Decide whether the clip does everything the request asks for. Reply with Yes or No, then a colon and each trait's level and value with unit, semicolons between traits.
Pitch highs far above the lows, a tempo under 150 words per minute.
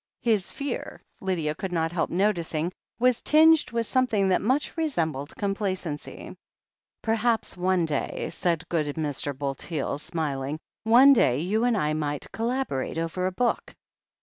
Yes: wide, 6.8 semitones; average, 140 wpm